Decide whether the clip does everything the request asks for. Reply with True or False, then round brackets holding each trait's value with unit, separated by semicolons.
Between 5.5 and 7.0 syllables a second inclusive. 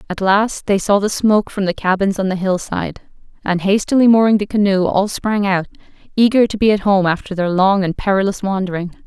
True (5.7 syllables/s)